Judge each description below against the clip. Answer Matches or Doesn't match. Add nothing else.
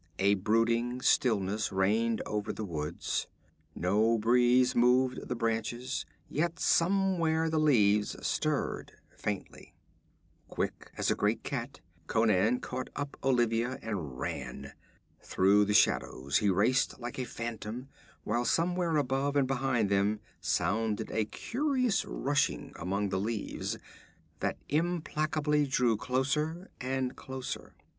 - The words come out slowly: Matches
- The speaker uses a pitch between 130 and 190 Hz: Doesn't match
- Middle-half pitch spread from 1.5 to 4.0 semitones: Doesn't match